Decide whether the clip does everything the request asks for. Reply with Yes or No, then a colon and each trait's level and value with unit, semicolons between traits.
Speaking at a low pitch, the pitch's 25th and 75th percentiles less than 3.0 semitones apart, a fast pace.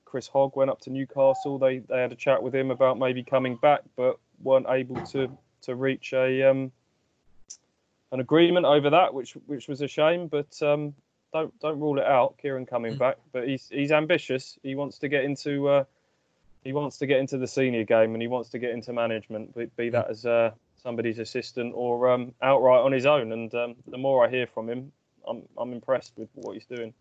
Yes: low, 130 Hz; narrow, 2.6 semitones; fast, 215 wpm